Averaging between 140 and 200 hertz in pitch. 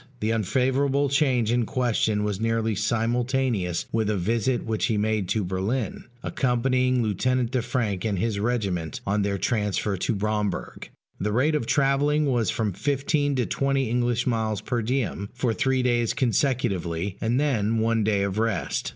No: low, 115 Hz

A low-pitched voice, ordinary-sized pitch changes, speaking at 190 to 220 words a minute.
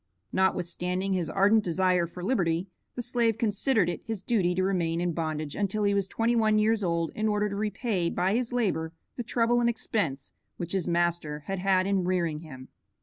No: high, 190 Hz; average, 4.0 semitones; average, 195 wpm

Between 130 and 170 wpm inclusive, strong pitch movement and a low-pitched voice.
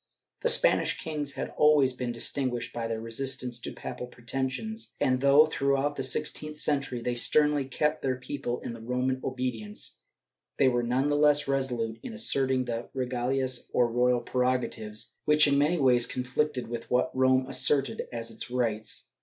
No: average, 165 wpm; narrow, 2.6 semitones; low, 130 Hz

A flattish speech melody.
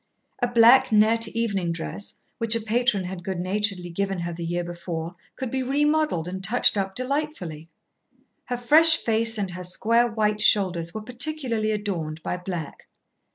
No: average, 5.1 semitones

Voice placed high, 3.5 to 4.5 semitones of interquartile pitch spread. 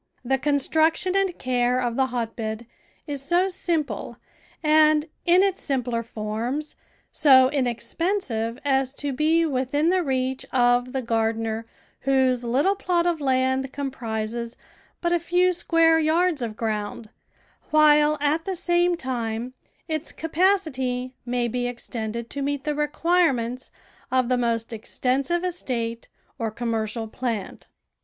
No: very high, 265 Hz; average, 4.9 semitones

